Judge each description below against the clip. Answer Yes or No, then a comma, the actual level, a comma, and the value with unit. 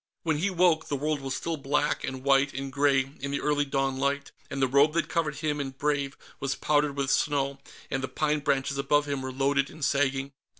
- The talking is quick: Yes, fast, 220 wpm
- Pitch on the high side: No, medium, 140 Hz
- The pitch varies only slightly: Yes, narrow, 1.6 semitones